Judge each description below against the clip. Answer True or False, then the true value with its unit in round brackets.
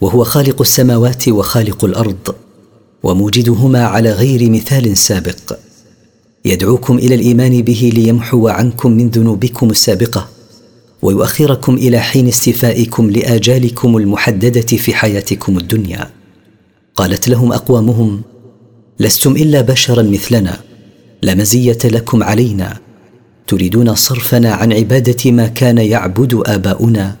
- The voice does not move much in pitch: True (2.2 semitones)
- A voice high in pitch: False (115 Hz)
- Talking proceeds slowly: False (105 wpm)